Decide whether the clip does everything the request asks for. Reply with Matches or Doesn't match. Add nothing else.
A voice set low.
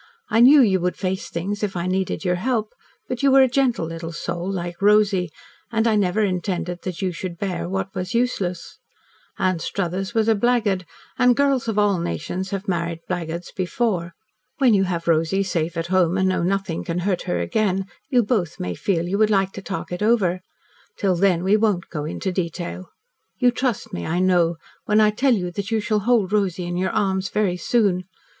Doesn't match